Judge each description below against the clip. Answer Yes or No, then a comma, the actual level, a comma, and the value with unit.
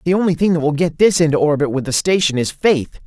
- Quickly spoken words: Yes, fast, 275 wpm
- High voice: No, medium, 160 Hz